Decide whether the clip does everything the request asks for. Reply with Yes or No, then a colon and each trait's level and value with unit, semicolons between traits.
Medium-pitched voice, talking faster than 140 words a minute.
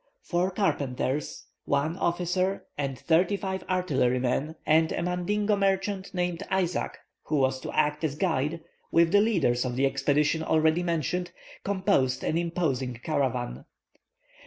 No: medium, 165 Hz; slow, 135 wpm